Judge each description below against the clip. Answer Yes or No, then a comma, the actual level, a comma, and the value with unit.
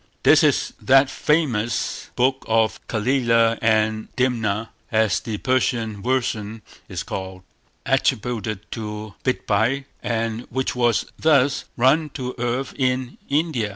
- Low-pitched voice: Yes, low, 120 Hz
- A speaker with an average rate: No, slow, 120 wpm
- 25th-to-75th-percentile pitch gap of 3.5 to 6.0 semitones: No, average, 3.0 semitones